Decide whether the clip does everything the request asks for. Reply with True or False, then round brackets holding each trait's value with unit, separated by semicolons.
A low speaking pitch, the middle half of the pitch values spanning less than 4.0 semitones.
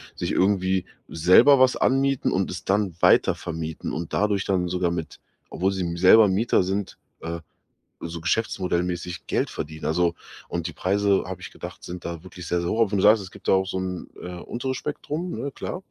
True (95 Hz; 2.9 semitones)